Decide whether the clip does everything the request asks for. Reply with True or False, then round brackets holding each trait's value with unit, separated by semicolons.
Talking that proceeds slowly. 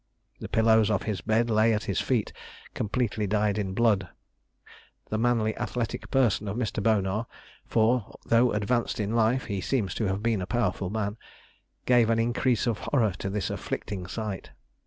False (170 wpm)